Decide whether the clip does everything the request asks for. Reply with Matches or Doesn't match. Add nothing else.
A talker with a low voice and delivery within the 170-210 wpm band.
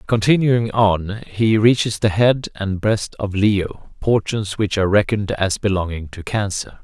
Doesn't match